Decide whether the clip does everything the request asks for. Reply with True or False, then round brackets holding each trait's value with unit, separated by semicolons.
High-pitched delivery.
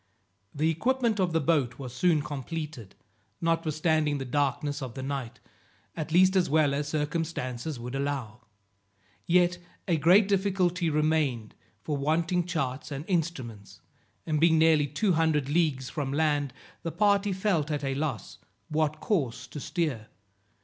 False (155 Hz)